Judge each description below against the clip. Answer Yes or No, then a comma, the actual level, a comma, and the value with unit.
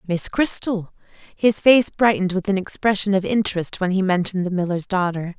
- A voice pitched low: No, high, 190 Hz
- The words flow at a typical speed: Yes, average, 180 wpm